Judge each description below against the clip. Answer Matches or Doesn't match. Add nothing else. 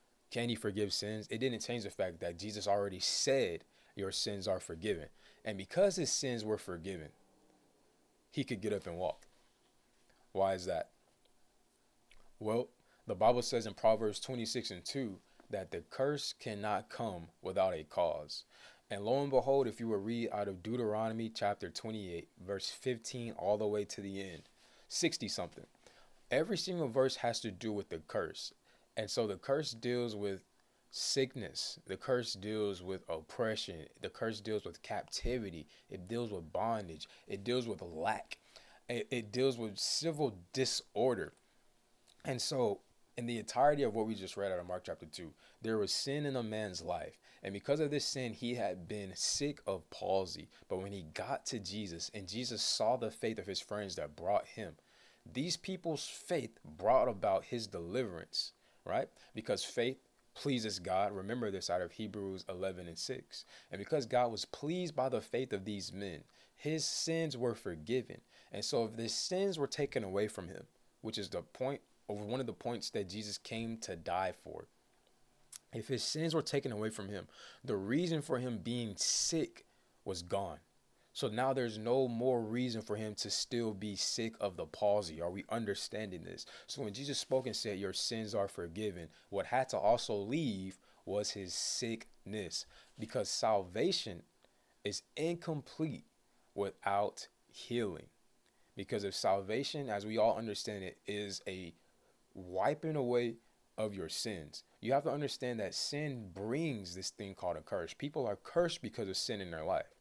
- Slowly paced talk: Doesn't match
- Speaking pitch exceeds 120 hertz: Doesn't match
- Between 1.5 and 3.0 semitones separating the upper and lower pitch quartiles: Doesn't match